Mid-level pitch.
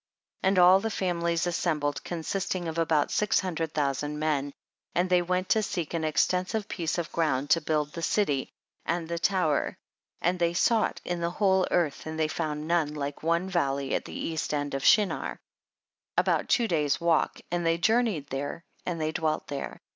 Yes: medium, 165 Hz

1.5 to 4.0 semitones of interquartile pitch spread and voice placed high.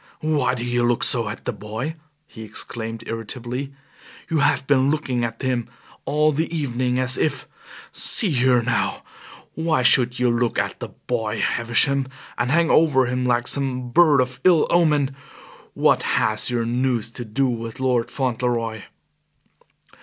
No: average, 2.8 semitones; low, 125 Hz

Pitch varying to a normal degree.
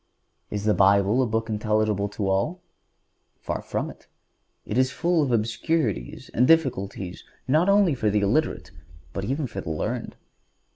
No: wide, 6.2 semitones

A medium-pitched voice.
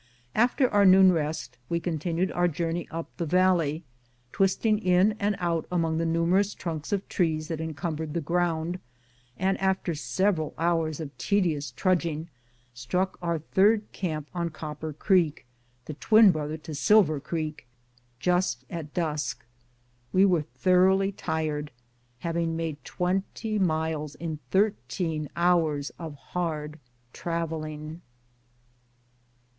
Yes: medium, 165 Hz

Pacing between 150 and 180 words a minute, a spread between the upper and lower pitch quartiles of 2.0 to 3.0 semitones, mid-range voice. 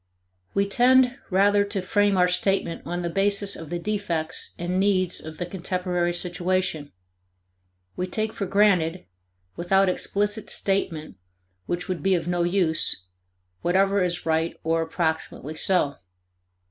No: slow, 135 wpm; average, 2.7 semitones; medium, 180 Hz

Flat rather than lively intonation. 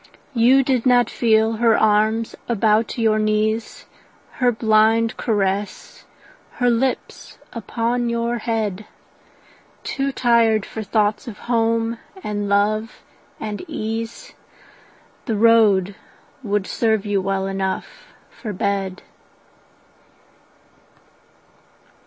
Yes: narrow, 2.0 semitones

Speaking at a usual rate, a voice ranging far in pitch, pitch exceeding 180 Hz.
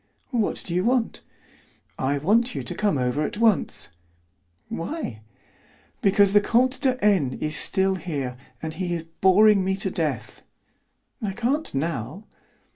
Yes: average, 145 wpm; wide, 6.0 semitones; high, 190 Hz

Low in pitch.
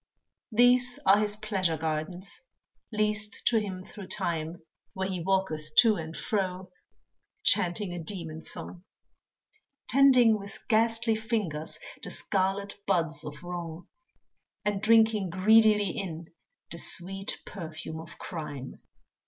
No: high, 190 Hz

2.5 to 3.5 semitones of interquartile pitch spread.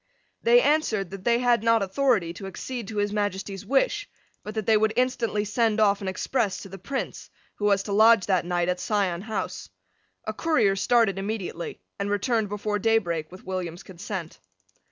Yes: average, 3.0 semitones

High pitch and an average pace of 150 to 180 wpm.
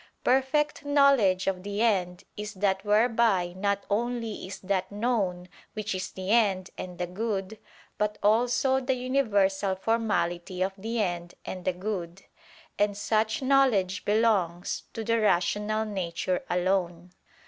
No: high, 205 Hz; slow, 135 wpm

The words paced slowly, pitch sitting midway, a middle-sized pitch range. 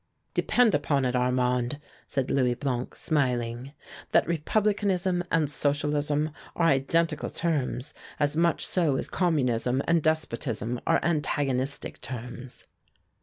Yes: slow, 115 wpm; medium, 145 Hz; average, 4.6 semitones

